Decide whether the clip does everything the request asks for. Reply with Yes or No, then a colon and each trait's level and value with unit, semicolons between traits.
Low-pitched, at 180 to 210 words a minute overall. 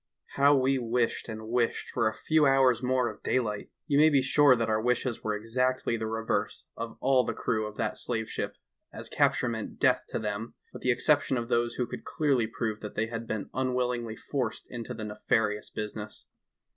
Yes: low, 115 Hz; average, 200 wpm